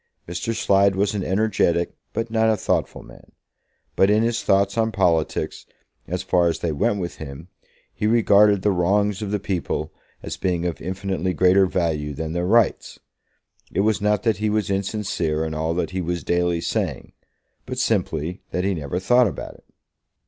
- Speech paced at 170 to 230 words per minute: Yes, average, 180 wpm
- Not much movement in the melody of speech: No, average, 3.3 semitones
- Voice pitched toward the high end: No, very low, 95 Hz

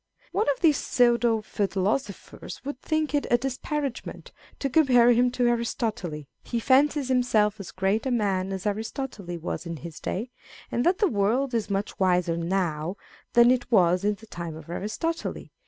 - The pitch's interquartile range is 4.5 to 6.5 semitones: Yes, average, 5.2 semitones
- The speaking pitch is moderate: No, high, 225 Hz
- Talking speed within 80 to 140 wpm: No, average, 170 wpm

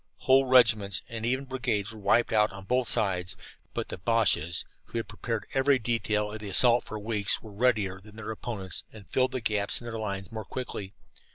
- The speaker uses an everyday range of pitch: Yes, average, 3.0 semitones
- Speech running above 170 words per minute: Yes, average, 200 wpm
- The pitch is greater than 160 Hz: No, low, 110 Hz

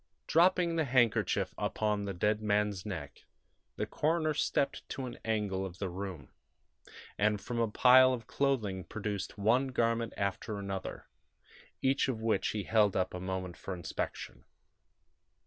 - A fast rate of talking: No, average, 145 wpm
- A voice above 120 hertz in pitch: No, low, 105 Hz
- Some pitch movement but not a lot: Yes, average, 4.5 semitones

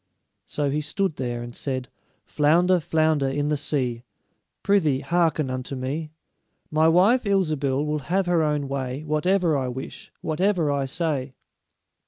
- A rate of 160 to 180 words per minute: No, average, 145 wpm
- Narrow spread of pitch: No, average, 3.8 semitones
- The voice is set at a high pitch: No, medium, 150 Hz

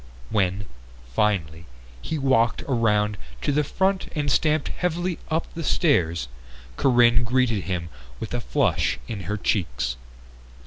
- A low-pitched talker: Yes, low, 115 Hz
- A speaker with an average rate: No, slow, 130 wpm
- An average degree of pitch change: No, wide, 7.6 semitones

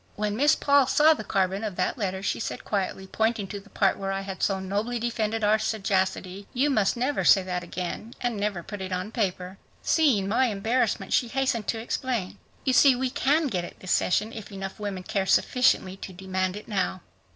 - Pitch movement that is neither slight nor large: Yes, average, 3.8 semitones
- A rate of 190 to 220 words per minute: Yes, fast, 205 wpm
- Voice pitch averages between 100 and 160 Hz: No, high, 205 Hz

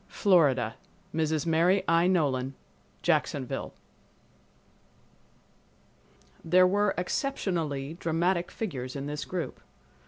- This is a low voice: No, medium, 165 Hz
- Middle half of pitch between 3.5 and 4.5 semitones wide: Yes, average, 4.2 semitones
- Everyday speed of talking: No, slow, 75 wpm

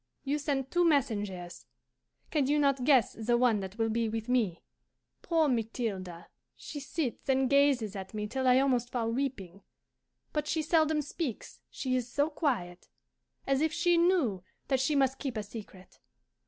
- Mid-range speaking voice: No, very high, 255 Hz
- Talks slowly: No, average, 170 wpm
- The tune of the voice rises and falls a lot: No, average, 4.7 semitones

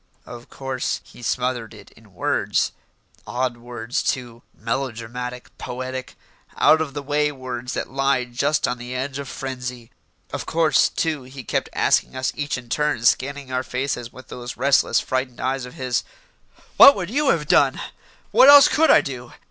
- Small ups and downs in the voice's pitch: Yes, narrow, 2.3 semitones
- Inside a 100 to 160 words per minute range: No, average, 170 wpm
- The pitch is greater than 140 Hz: No, low, 130 Hz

